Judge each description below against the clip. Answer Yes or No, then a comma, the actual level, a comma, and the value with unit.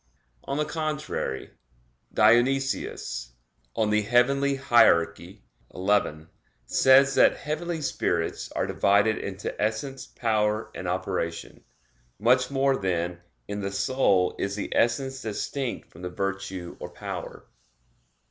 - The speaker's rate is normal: No, slow, 110 wpm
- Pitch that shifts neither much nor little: No, wide, 5.9 semitones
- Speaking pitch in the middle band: No, low, 110 Hz